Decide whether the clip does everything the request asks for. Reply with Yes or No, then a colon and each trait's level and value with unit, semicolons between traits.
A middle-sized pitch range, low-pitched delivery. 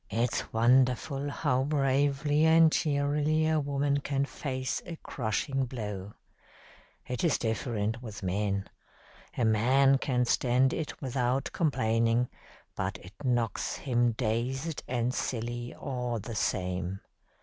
Yes: average, 3.6 semitones; low, 125 Hz